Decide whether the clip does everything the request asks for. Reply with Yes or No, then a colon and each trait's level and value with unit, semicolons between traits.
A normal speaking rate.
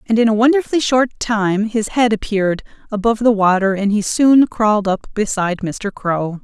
Yes: average, 185 wpm